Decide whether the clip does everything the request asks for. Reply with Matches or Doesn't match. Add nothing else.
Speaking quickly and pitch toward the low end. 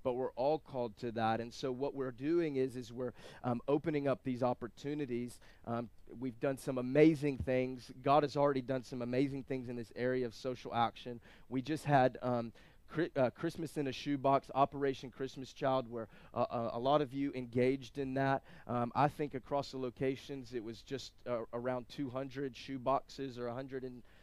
Doesn't match